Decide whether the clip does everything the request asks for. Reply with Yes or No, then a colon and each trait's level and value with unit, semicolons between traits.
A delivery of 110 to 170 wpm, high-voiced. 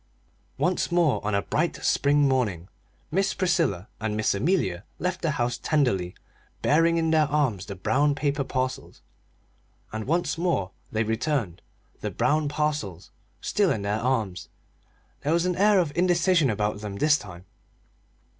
No: average, 150 wpm; medium, 140 Hz